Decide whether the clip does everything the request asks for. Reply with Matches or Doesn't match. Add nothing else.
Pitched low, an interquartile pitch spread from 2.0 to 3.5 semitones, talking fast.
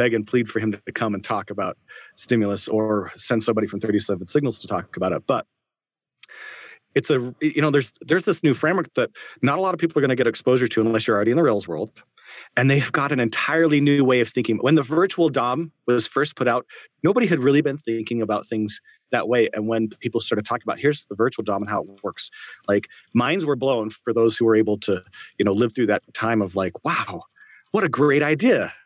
Doesn't match